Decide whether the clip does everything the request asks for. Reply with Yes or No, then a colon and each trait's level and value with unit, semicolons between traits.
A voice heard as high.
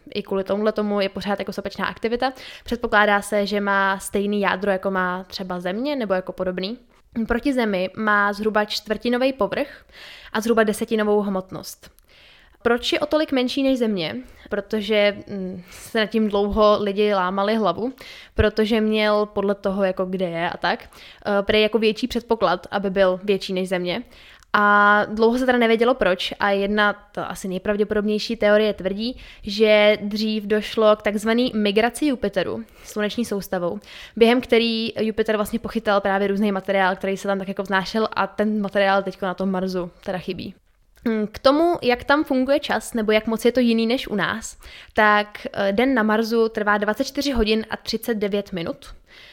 Yes: high, 210 Hz